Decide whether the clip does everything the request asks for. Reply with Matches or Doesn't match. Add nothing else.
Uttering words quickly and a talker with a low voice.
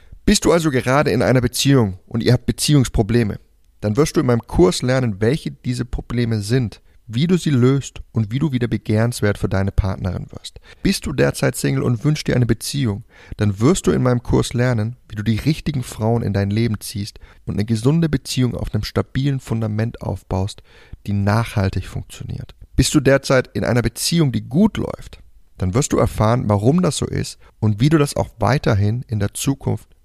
Matches